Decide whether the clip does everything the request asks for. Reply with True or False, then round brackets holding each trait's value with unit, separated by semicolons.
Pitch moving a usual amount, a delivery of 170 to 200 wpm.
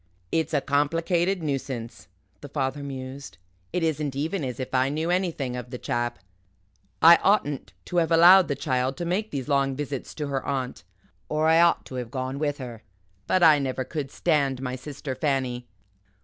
True (3.7 semitones; 180 wpm)